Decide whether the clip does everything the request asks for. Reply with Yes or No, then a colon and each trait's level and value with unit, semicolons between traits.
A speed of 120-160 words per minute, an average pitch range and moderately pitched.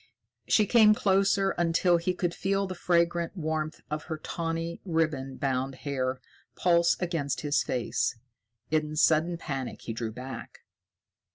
Yes: average, 140 wpm; average, 3.8 semitones; medium, 165 Hz